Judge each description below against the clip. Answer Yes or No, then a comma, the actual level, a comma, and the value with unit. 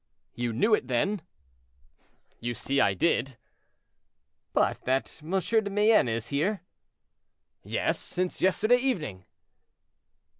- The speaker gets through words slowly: Yes, slow, 110 wpm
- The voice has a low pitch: No, medium, 165 Hz